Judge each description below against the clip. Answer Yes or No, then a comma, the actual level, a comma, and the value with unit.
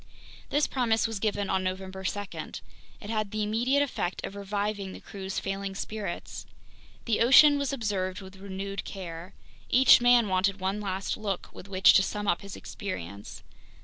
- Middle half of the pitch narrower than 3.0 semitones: Yes, narrow, 2.4 semitones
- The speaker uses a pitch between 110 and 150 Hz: No, high, 200 Hz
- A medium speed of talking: Yes, average, 165 wpm